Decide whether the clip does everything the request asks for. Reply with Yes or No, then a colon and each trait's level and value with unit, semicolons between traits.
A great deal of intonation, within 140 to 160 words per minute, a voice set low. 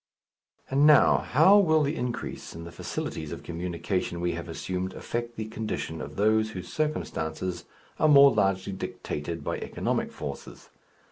Yes: wide, 7.9 semitones; average, 150 wpm; low, 105 Hz